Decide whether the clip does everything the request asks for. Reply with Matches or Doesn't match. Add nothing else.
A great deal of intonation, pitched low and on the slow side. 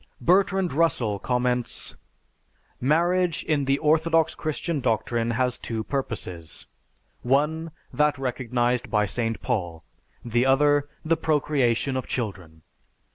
Doesn't match